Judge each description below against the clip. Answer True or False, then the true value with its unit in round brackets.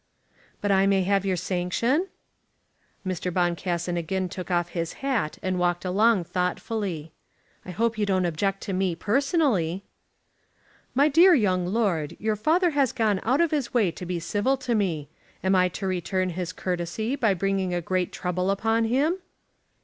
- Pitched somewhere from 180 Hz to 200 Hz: True (190 Hz)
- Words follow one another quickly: False (165 wpm)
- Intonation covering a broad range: False (4.1 semitones)